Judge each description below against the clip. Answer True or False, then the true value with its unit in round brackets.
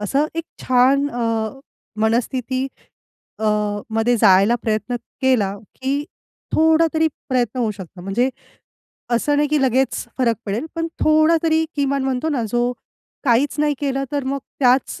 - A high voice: True (260 Hz)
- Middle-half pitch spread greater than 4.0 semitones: False (3.7 semitones)